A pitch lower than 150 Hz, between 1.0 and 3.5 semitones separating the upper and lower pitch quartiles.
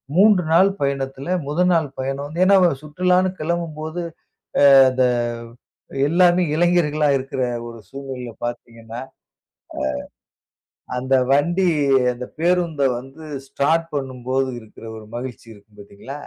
No: medium, 140 Hz; average, 5.0 semitones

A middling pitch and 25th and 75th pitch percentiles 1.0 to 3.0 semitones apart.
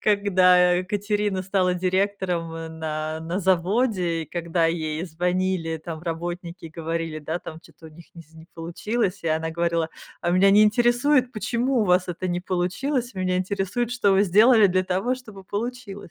No: medium, 180 Hz; average, 3.4 semitones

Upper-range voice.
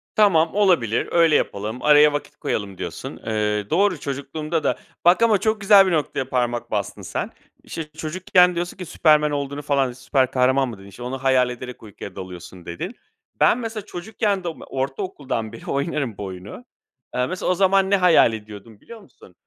No: medium, 140 Hz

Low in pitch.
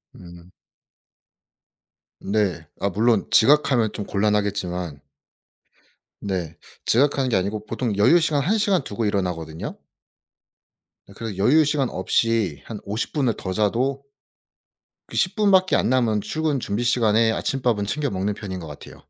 Yes: low, 110 Hz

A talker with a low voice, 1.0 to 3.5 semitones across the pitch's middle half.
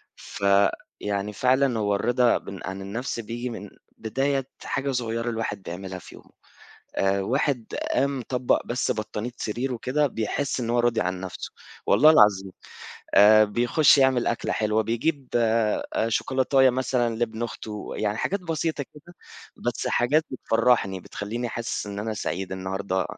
No: low, 115 Hz; average, 3.9 semitones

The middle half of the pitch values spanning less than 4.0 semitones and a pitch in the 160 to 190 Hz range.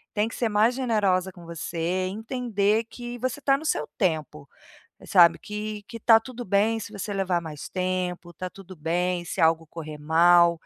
No: average, 4.5 semitones; medium, 185 Hz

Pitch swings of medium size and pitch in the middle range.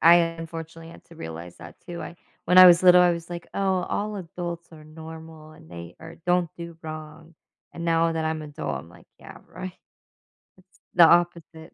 No: narrow, 1.6 semitones; medium, 165 Hz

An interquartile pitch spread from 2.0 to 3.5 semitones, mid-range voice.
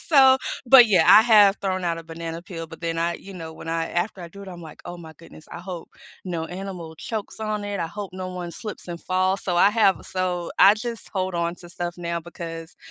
Yes: average, 2.9 semitones; medium, 180 Hz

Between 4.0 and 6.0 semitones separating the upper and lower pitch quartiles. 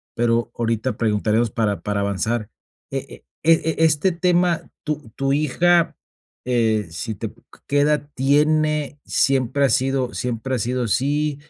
Yes: average, 4.7 semitones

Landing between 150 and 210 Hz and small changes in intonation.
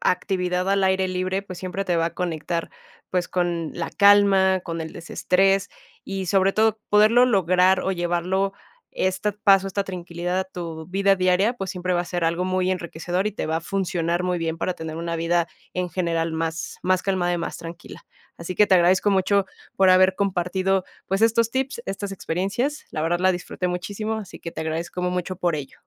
Yes: medium, 185 Hz; narrow, 2.1 semitones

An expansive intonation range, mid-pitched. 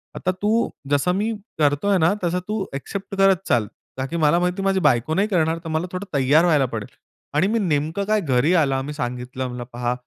Yes: wide, 6.0 semitones; medium, 160 Hz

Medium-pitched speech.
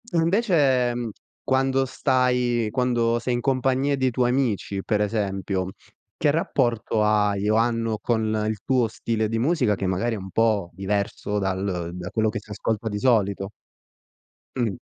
No: low, 115 Hz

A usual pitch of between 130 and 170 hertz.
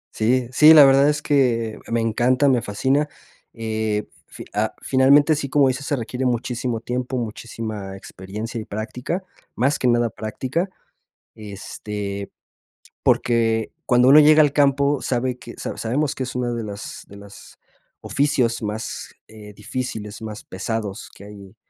No: low, 120 Hz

